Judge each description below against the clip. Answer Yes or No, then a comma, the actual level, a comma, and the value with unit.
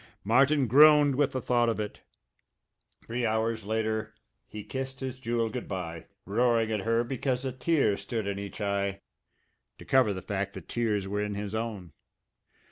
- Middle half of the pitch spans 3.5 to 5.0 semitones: Yes, average, 3.8 semitones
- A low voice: Yes, low, 110 Hz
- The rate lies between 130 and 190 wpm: Yes, average, 170 wpm